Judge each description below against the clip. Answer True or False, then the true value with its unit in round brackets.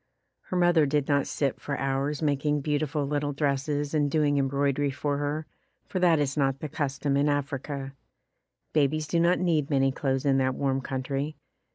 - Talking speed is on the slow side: False (175 wpm)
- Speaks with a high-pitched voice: False (145 Hz)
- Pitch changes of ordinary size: False (1.6 semitones)